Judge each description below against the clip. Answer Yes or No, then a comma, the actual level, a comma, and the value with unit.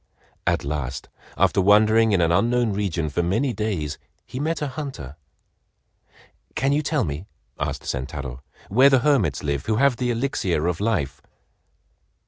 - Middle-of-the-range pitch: No, low, 105 Hz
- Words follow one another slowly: No, average, 150 wpm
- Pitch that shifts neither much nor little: No, wide, 8.9 semitones